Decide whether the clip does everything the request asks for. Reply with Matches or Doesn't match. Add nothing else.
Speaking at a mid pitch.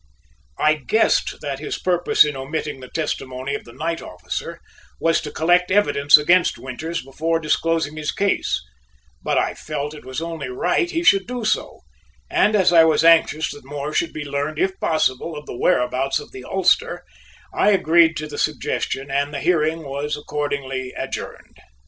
Matches